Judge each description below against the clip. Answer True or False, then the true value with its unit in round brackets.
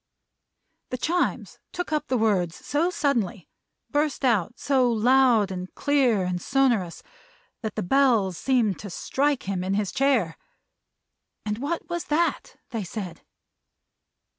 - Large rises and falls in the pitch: True (6.3 semitones)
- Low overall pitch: False (240 Hz)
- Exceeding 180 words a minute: False (135 wpm)